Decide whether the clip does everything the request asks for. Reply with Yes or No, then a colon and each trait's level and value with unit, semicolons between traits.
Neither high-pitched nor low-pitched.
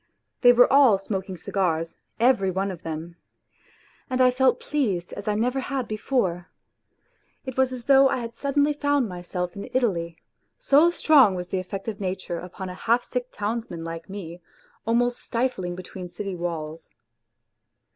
No: high, 205 Hz